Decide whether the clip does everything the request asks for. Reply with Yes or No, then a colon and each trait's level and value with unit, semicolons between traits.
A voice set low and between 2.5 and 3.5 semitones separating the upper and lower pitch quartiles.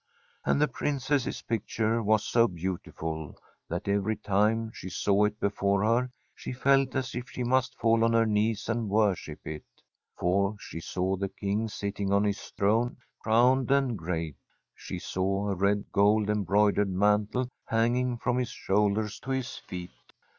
Yes: low, 105 Hz; average, 3.1 semitones